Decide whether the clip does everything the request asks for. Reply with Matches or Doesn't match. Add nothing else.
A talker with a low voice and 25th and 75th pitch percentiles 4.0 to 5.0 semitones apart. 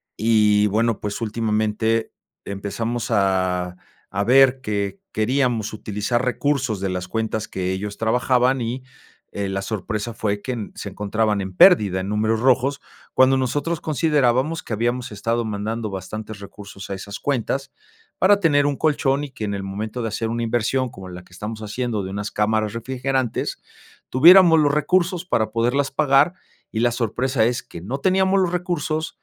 Matches